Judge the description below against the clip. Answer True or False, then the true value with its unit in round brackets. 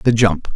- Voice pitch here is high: False (105 Hz)